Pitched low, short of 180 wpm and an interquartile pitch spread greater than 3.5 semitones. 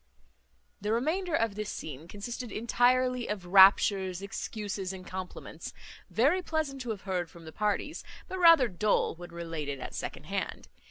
No: high, 210 Hz; average, 155 wpm; wide, 5.5 semitones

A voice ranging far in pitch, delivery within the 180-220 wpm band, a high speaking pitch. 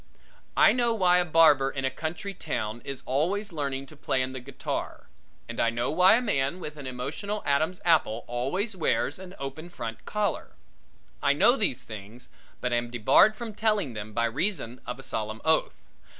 No: wide, 6.9 semitones; average, 185 wpm; medium, 140 Hz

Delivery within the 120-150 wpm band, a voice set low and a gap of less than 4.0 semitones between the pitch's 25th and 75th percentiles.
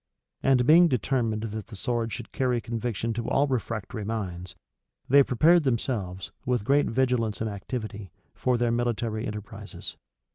Yes: average, 145 wpm; low, 115 Hz; average, 2.8 semitones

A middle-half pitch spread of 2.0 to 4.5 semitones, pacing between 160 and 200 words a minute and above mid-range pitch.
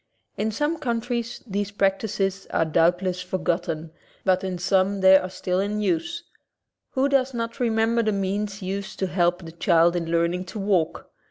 Yes: average, 3.7 semitones; average, 170 wpm; high, 195 Hz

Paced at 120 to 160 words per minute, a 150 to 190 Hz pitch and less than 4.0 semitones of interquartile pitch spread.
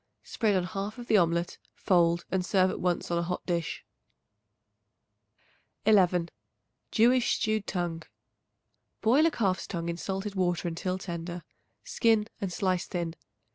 Yes: average, 140 wpm; medium, 185 Hz; average, 3.3 semitones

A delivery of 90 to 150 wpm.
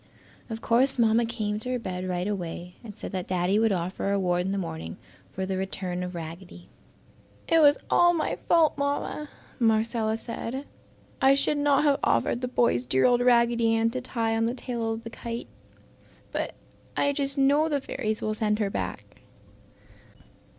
No: average, 180 wpm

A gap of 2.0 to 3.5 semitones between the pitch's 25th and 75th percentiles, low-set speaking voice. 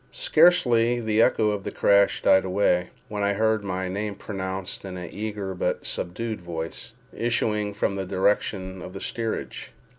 Yes: average, 2.7 semitones; low, 100 Hz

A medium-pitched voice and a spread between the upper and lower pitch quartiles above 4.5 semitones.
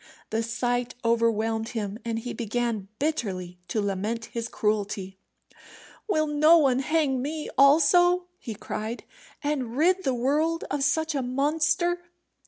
No: very high, 250 Hz; average, 5.3 semitones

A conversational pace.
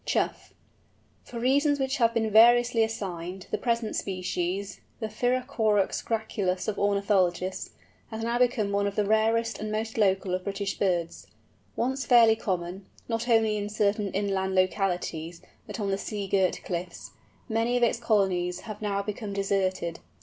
Yes: average, 155 wpm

